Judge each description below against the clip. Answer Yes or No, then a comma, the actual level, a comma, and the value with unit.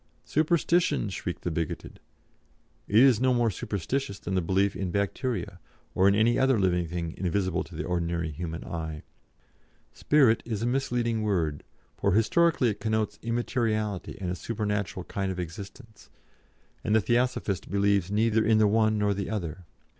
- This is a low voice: Yes, low, 100 Hz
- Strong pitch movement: No, average, 4.1 semitones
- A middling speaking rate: Yes, average, 160 wpm